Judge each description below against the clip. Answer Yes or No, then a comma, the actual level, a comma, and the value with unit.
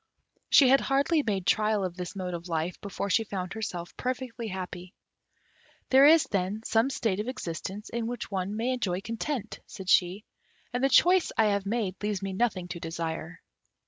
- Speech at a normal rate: Yes, average, 180 wpm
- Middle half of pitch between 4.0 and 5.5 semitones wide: Yes, average, 4.6 semitones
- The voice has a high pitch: Yes, high, 205 Hz